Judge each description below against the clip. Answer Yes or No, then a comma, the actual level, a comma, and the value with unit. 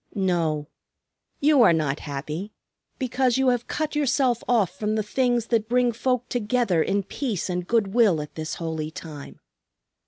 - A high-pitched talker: Yes, high, 215 Hz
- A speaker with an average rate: Yes, average, 160 wpm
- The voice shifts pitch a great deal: Yes, wide, 7.0 semitones